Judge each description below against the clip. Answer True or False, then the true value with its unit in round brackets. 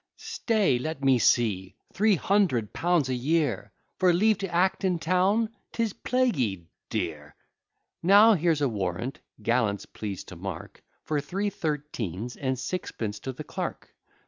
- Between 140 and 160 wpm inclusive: True (145 wpm)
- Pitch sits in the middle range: True (150 Hz)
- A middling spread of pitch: False (8.4 semitones)